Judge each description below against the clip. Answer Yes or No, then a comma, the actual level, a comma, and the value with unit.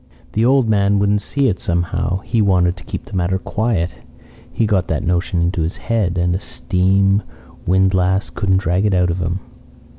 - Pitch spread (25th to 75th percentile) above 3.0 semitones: No, narrow, 2.4 semitones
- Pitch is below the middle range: Yes, very low, 95 Hz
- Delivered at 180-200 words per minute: Yes, average, 185 wpm